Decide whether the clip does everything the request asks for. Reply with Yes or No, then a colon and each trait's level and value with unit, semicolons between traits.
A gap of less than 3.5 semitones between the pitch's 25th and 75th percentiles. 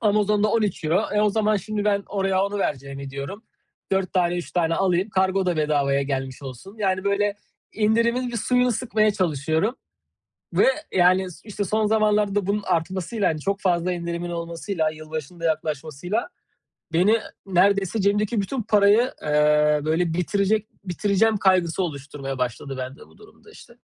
No: average, 4.7 semitones